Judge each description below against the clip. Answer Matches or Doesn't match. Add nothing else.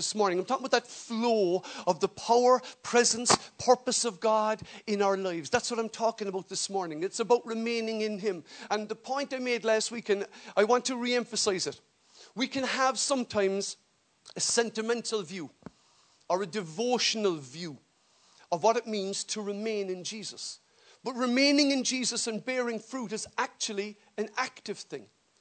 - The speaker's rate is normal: Matches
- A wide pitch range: Doesn't match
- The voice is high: Matches